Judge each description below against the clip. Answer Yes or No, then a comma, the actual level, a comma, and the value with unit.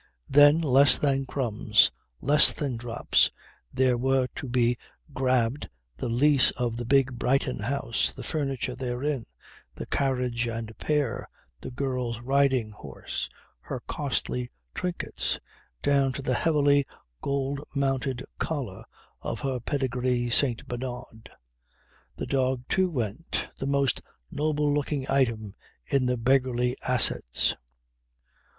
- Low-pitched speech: Yes, low, 130 Hz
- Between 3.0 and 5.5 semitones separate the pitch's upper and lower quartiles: No, narrow, 2.5 semitones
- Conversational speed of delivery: No, slow, 120 wpm